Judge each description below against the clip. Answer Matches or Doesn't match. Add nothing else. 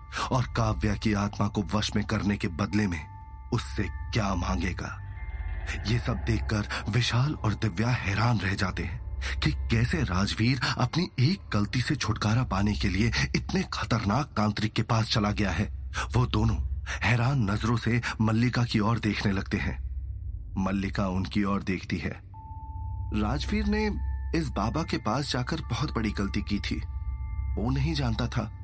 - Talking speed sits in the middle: Matches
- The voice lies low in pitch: Matches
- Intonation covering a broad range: Doesn't match